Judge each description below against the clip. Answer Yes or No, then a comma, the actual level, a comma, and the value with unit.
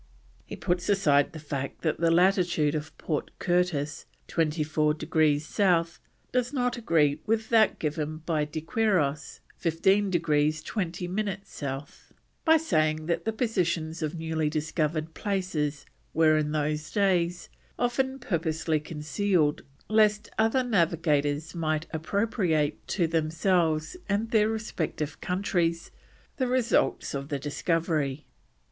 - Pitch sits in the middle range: Yes, medium, 165 Hz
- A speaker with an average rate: No, slow, 125 wpm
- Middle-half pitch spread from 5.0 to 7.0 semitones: No, average, 4.3 semitones